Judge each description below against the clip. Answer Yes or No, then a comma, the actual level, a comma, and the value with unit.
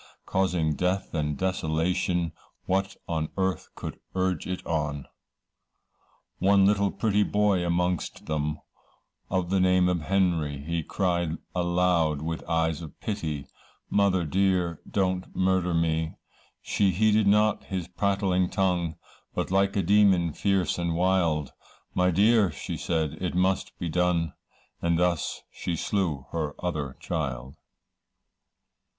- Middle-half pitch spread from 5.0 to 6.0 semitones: No, average, 2.8 semitones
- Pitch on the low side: Yes, very low, 90 Hz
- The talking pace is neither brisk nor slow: No, slow, 130 wpm